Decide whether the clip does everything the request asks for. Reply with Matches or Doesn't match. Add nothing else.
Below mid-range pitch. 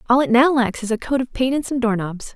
Doesn't match